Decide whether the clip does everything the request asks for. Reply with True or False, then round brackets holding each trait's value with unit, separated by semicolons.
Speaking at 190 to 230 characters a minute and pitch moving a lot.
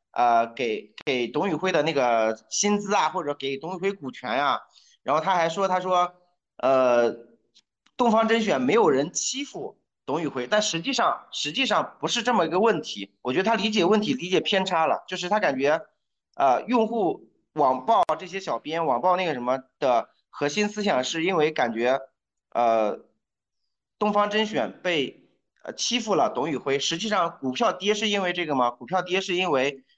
False (260 characters per minute; 7.7 semitones)